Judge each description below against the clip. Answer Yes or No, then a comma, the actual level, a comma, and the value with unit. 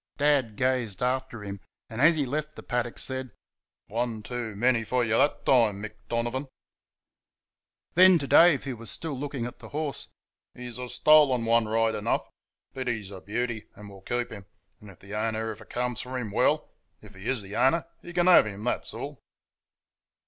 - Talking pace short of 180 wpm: No, average, 190 wpm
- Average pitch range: Yes, average, 3.4 semitones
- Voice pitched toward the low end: Yes, low, 120 Hz